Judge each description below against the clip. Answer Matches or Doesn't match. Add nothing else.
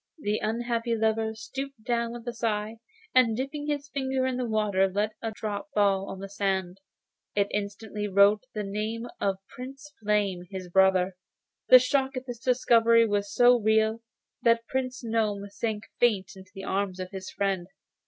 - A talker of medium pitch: Doesn't match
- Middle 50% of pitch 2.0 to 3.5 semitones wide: Matches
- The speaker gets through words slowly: Doesn't match